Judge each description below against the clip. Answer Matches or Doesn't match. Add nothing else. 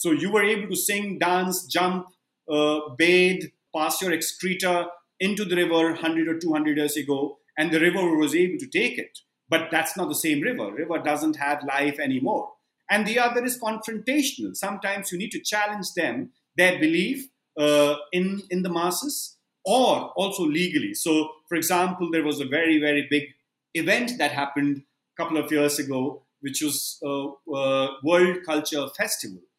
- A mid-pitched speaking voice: Matches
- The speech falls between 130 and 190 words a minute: Matches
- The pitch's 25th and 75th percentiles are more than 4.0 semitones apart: Matches